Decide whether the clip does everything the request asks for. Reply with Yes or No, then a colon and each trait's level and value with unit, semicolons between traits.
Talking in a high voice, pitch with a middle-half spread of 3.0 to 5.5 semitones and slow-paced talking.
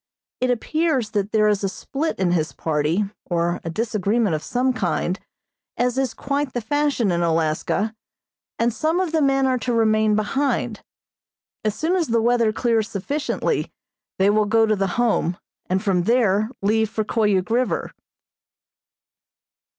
No: high, 220 Hz; average, 4.4 semitones; average, 160 wpm